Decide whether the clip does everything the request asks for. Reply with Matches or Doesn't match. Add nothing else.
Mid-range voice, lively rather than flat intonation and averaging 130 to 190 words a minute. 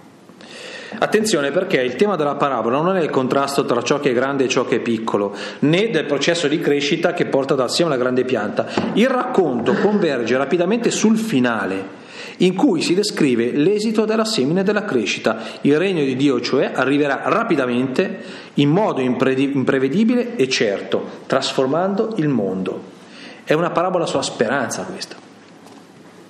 Matches